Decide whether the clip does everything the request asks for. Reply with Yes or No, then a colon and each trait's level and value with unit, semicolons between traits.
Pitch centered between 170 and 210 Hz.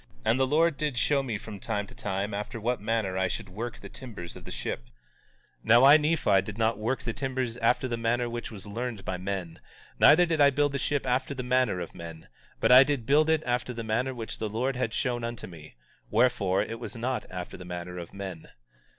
No: low, 115 Hz